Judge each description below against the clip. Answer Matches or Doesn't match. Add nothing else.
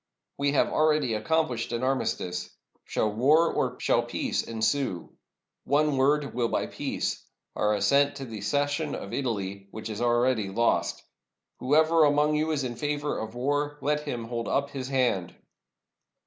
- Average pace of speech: Matches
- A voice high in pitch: Doesn't match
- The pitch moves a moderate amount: Matches